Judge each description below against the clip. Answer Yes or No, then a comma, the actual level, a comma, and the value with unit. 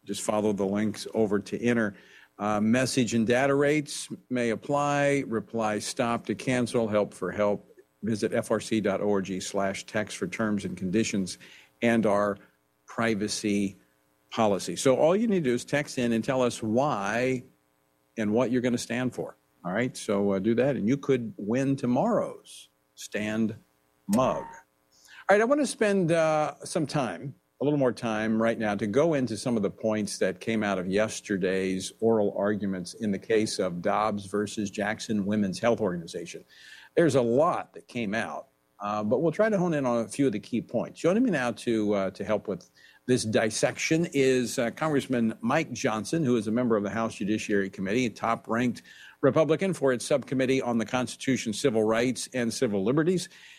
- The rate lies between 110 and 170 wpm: No, average, 185 wpm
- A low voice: Yes, low, 115 Hz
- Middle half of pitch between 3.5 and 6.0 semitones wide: Yes, average, 4.2 semitones